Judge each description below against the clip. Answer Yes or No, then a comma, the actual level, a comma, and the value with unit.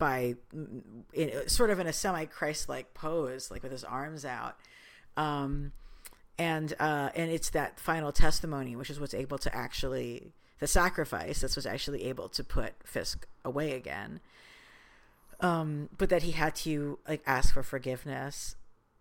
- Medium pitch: Yes, medium, 145 Hz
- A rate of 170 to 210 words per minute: No, average, 160 wpm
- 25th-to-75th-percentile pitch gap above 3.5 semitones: No, average, 3.1 semitones